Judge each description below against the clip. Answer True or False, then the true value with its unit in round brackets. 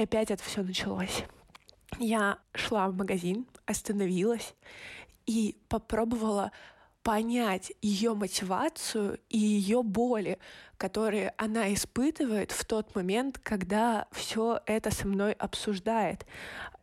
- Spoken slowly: True (105 wpm)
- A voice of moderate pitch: False (215 Hz)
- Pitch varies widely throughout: False (2.4 semitones)